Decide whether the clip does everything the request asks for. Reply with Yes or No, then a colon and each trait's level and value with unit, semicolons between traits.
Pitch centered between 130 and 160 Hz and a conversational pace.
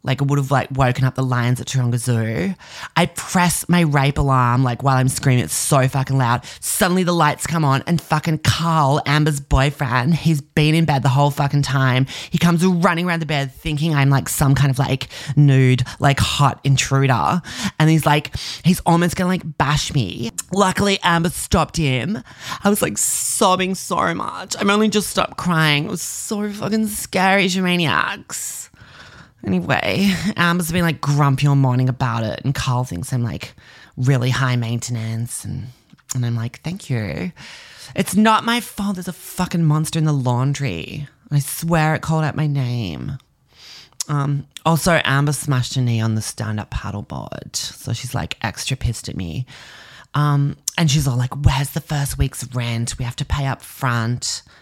Yes: medium, 140 Hz; average, 180 wpm